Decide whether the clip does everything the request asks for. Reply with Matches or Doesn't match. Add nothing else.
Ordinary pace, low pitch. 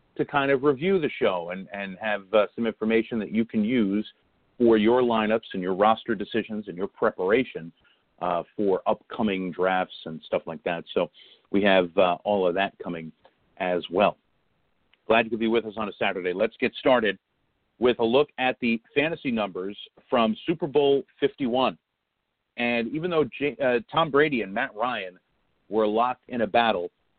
Matches